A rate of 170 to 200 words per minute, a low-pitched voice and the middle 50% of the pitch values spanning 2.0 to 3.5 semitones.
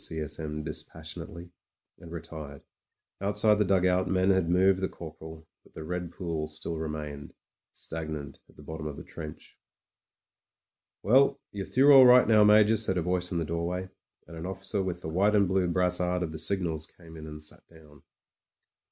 Yes: average, 185 wpm; very low, 85 Hz; average, 3.1 semitones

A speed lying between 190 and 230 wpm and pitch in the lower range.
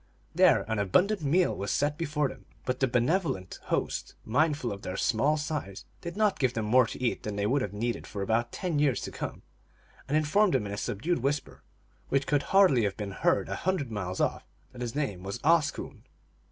Yes: fast, 205 wpm; low, 130 Hz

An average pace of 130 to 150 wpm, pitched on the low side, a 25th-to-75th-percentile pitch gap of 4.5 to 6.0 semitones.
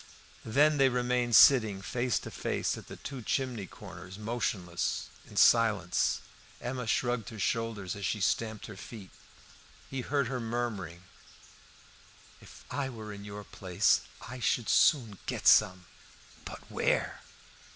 No: average, 140 wpm; low, 115 Hz; average, 3.6 semitones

